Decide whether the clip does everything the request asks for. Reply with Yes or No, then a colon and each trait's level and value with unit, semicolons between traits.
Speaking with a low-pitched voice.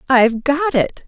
No: very high, 270 Hz